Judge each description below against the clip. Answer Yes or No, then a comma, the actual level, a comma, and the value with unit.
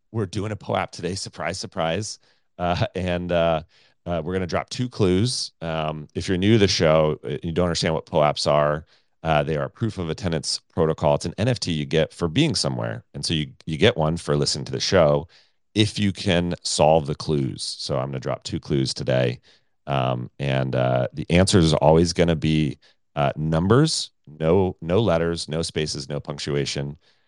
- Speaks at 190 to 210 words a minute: Yes, average, 200 wpm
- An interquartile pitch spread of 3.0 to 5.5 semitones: Yes, average, 3.9 semitones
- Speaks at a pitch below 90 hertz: Yes, very low, 80 Hz